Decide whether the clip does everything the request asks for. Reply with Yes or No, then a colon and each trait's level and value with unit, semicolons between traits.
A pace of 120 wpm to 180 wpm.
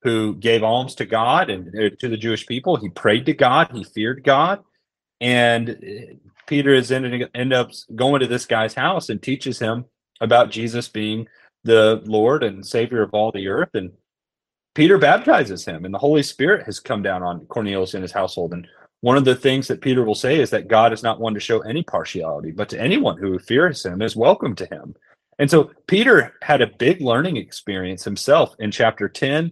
No: average, 200 wpm